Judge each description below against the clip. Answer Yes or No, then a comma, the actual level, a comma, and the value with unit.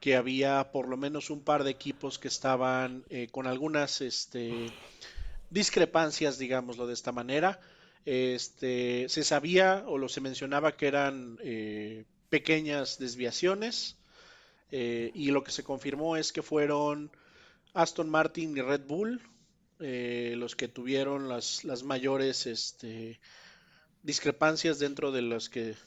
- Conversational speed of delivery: Yes, average, 135 wpm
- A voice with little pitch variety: No, average, 3.6 semitones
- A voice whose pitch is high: No, low, 135 Hz